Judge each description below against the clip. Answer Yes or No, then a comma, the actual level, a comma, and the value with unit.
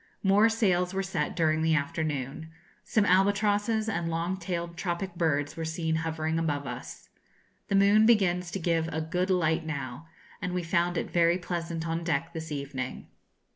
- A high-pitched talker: No, medium, 170 Hz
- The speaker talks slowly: No, average, 170 wpm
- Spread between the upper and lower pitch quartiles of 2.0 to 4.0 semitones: Yes, average, 2.7 semitones